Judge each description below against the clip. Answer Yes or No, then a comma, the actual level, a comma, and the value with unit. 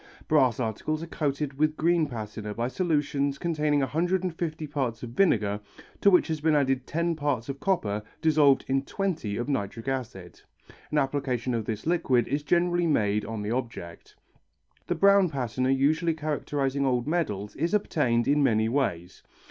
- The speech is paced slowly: No, average, 165 wpm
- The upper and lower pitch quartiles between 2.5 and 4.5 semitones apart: No, average, 5.1 semitones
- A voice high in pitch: No, medium, 140 Hz